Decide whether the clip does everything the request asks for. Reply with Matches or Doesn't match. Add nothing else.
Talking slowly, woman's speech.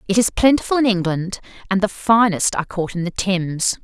Doesn't match